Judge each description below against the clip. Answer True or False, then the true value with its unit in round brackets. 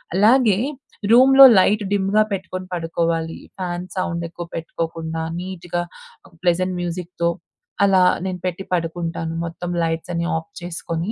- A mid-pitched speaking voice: True (175 Hz)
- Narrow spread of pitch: True (2.1 semitones)